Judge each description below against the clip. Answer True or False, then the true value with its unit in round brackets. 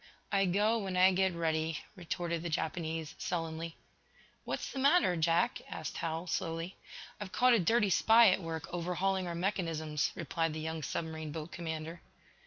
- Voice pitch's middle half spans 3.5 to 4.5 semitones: False (2.8 semitones)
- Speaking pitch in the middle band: True (170 Hz)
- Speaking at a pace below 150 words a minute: False (160 wpm)